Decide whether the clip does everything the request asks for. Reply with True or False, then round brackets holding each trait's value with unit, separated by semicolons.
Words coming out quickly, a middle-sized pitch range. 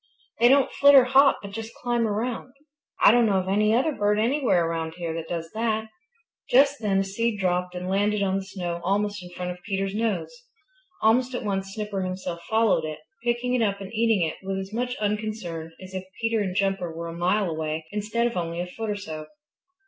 True (215 wpm; 4.0 semitones)